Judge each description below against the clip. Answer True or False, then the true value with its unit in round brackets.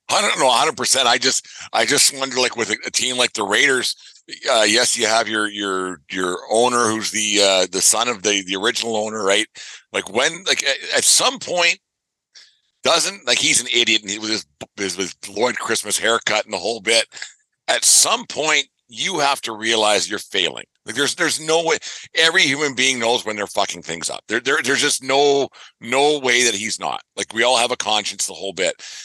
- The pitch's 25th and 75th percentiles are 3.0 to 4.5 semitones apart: False (5.0 semitones)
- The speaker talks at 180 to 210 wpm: True (205 wpm)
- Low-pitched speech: True (115 Hz)